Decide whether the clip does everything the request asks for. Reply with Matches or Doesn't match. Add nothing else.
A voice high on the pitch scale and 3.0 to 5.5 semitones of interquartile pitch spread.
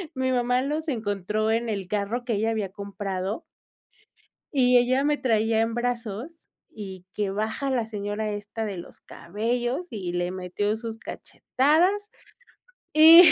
Matches